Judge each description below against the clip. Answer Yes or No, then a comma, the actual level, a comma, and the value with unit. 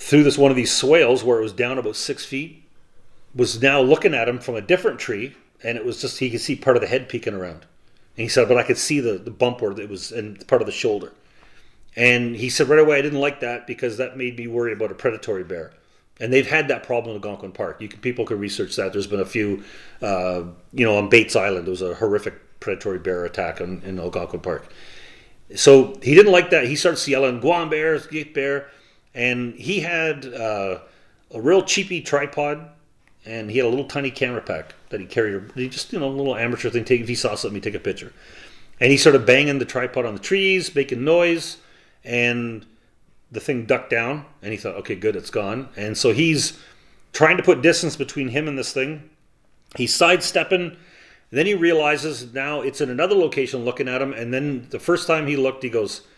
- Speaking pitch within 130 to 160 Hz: Yes, low, 135 Hz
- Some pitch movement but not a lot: Yes, average, 4.6 semitones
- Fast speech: Yes, fast, 225 wpm